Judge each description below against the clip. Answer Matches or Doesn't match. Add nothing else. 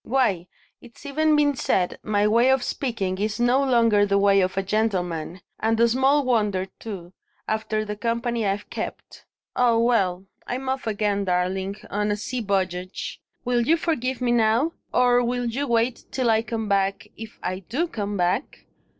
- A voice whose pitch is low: Doesn't match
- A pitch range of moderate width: Matches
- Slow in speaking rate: Doesn't match